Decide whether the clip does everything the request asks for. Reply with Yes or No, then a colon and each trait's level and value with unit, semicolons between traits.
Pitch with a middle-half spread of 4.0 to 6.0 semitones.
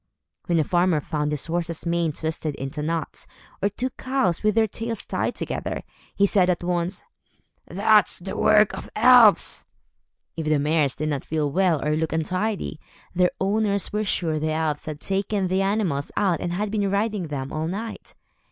Yes: average, 4.6 semitones